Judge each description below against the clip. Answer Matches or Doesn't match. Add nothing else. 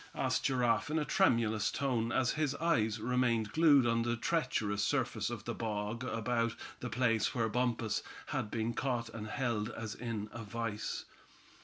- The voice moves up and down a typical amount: Doesn't match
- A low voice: Matches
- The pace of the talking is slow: Doesn't match